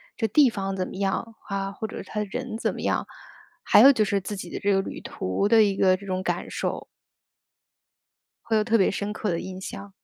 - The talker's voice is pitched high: Yes, high, 200 Hz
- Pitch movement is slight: Yes, narrow, 2.2 semitones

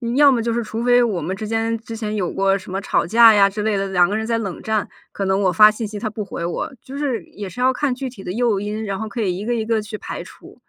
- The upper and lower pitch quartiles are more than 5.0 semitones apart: No, average, 2.8 semitones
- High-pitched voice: Yes, high, 215 Hz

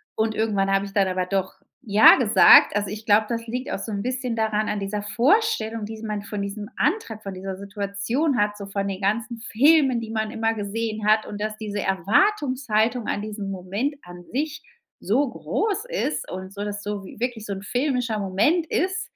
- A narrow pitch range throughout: No, average, 3.5 semitones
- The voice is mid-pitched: No, high, 215 Hz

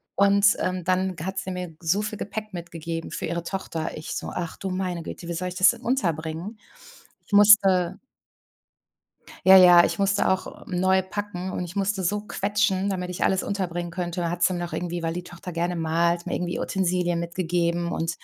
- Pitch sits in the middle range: Yes, medium, 180 Hz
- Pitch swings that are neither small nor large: No, narrow, 2.1 semitones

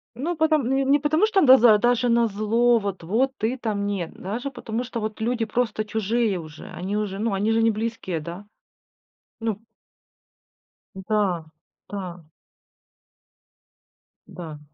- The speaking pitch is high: Yes, high, 220 Hz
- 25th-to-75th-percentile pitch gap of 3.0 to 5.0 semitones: Yes, average, 3.5 semitones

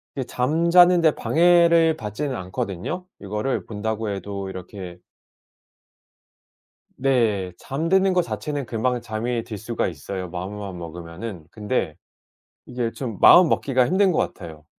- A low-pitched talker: Yes, low, 115 Hz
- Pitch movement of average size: No, wide, 7.7 semitones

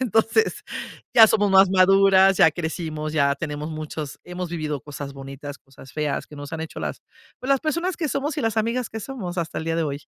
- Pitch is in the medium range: Yes, medium, 170 Hz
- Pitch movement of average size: No, wide, 6.7 semitones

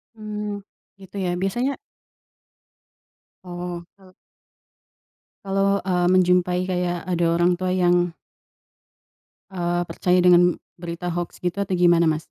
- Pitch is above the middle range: No, medium, 180 Hz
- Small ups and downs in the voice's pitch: Yes, narrow, 1.3 semitones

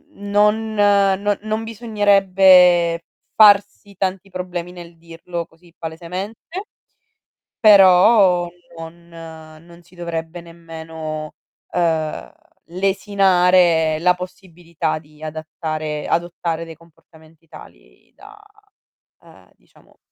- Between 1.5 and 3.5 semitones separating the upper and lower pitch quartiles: Yes, average, 2.9 semitones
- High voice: No, medium, 175 Hz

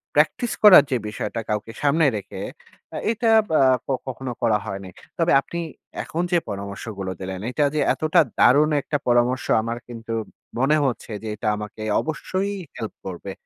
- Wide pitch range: Yes, wide, 6.4 semitones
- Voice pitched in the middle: No, low, 120 Hz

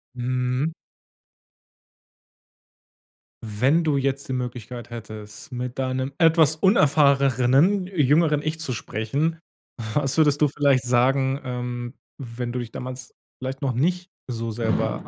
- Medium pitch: No, low, 130 Hz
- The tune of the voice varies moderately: Yes, average, 3.3 semitones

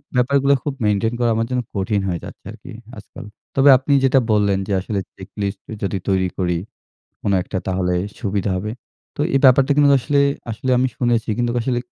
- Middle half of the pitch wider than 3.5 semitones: Yes, average, 4.8 semitones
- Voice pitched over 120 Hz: No, low, 110 Hz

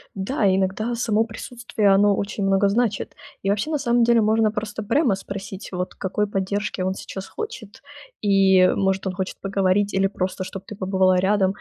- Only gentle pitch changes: Yes, narrow, 2.3 semitones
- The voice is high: Yes, high, 200 Hz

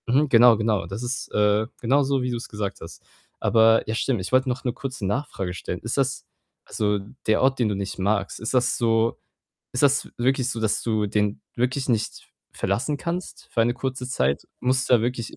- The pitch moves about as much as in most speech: Yes, average, 3.4 semitones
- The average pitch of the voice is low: Yes, low, 120 Hz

